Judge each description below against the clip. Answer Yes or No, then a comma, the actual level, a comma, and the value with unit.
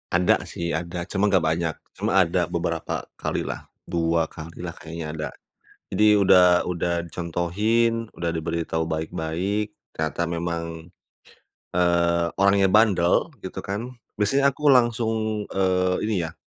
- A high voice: No, very low, 90 Hz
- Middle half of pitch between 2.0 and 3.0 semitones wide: No, average, 3.6 semitones